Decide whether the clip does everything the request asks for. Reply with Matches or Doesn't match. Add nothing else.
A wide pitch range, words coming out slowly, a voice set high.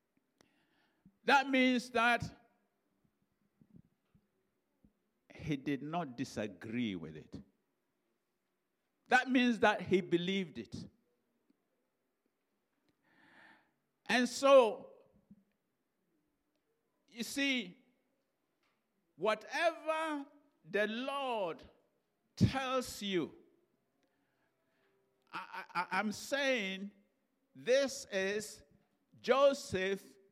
Matches